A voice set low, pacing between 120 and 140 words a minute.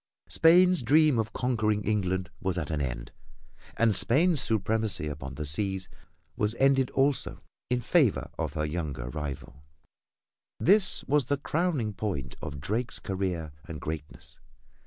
Yes: low, 105 Hz; slow, 135 wpm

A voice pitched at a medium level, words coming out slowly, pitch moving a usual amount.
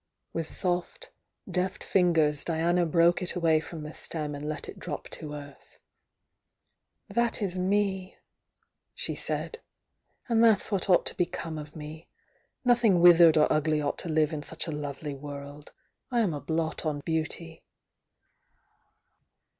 No: medium, 165 Hz; average, 145 wpm; average, 3.1 semitones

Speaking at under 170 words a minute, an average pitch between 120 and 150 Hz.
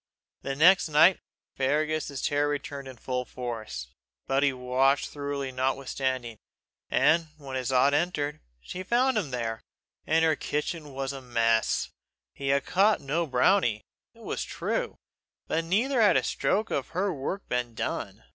Yes: average, 155 wpm; medium, 140 Hz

